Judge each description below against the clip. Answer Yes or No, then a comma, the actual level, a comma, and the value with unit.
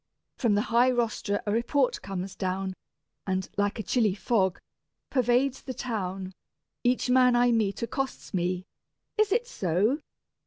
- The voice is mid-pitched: No, high, 220 Hz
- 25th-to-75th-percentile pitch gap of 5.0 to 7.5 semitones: No, average, 4.6 semitones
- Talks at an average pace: Yes, average, 145 wpm